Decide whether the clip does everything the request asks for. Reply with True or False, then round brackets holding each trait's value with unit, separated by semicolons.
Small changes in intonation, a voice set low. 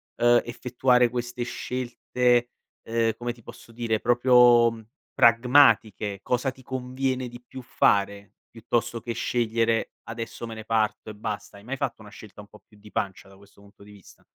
True (2.3 semitones; 115 Hz)